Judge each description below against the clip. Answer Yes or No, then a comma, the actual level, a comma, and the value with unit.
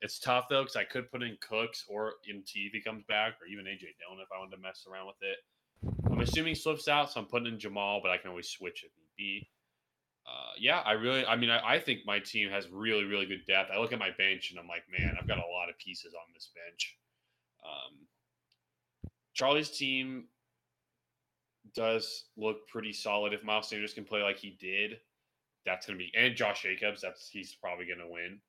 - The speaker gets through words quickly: Yes, fast, 225 wpm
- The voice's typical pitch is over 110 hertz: No, low, 105 Hz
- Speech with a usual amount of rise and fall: Yes, average, 3.1 semitones